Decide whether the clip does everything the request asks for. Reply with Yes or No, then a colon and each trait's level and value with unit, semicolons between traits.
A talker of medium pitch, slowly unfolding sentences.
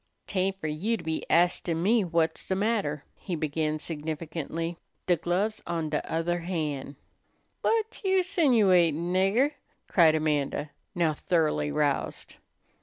Yes: medium, 170 Hz; slow, 130 wpm